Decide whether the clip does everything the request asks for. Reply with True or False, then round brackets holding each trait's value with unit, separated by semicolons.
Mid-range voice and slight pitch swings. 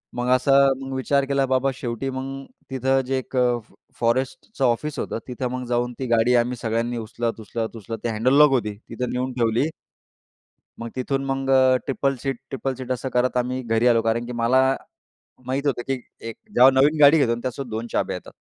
False (125 Hz; 2.3 semitones)